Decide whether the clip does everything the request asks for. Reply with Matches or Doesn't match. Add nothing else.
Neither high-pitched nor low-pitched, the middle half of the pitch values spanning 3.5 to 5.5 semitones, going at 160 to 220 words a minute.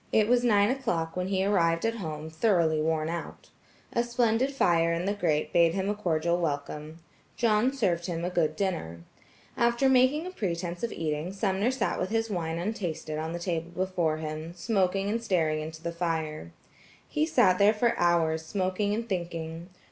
Matches